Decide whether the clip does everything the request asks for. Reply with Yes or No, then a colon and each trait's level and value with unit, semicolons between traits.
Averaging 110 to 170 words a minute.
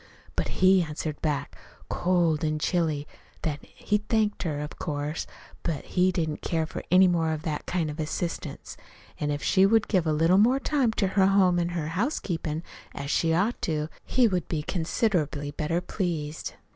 No: average, 180 wpm